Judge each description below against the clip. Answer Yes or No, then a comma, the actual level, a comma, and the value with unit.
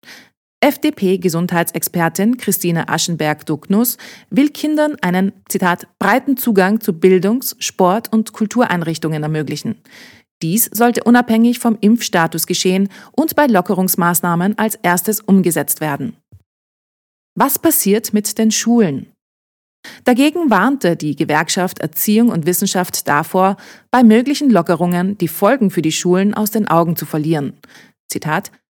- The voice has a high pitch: Yes, high, 195 Hz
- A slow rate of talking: Yes, slow, 115 wpm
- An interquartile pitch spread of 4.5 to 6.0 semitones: Yes, average, 5.1 semitones